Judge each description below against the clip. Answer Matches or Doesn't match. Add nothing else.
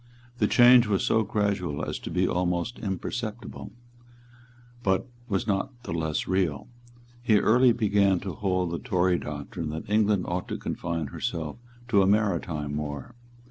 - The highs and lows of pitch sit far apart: Doesn't match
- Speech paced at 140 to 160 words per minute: Matches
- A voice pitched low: Matches